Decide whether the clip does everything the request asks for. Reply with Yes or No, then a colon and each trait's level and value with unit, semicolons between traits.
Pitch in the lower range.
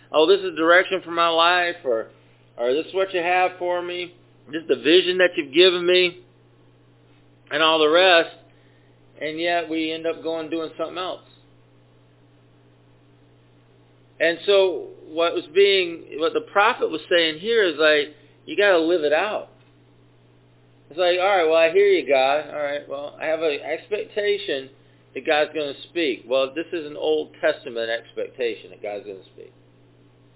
No: medium, 160 Hz